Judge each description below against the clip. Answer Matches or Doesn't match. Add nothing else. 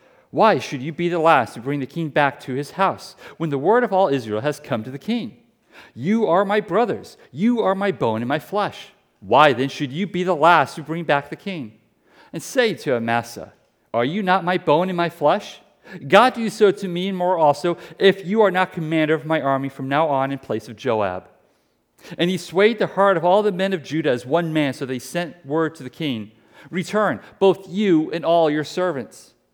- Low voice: Doesn't match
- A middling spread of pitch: Matches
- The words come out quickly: Matches